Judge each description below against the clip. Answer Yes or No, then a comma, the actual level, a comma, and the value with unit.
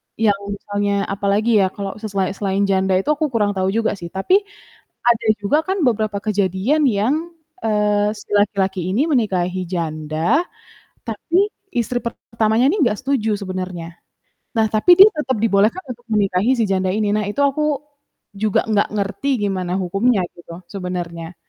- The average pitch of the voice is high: Yes, high, 205 Hz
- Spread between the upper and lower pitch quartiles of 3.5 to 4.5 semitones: Yes, average, 3.8 semitones